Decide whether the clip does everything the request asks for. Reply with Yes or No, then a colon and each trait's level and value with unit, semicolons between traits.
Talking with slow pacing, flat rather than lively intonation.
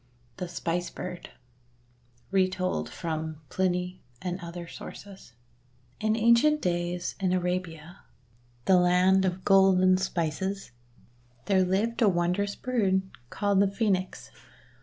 Yes: slow, 115 wpm; narrow, 1.7 semitones